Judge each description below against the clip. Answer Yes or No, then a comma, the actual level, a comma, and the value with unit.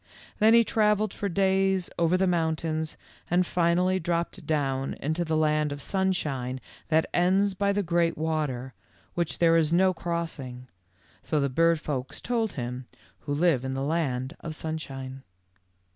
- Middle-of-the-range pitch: Yes, medium, 165 Hz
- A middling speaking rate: Yes, average, 155 wpm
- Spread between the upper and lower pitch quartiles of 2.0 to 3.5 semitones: No, average, 4.3 semitones